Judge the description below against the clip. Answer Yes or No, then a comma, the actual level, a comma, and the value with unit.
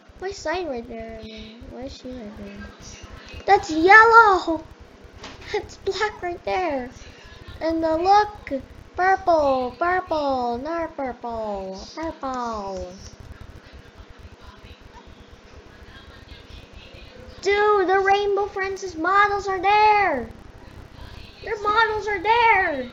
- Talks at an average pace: No, slow, 85 wpm